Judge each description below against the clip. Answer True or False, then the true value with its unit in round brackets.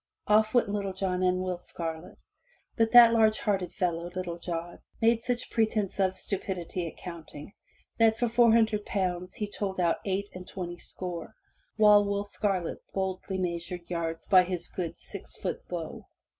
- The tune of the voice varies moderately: True (3.1 semitones)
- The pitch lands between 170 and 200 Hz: True (190 Hz)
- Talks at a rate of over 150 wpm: True (170 wpm)